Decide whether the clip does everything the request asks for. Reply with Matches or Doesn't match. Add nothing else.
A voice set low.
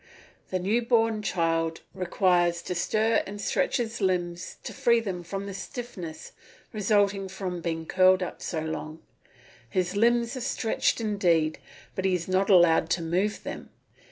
Doesn't match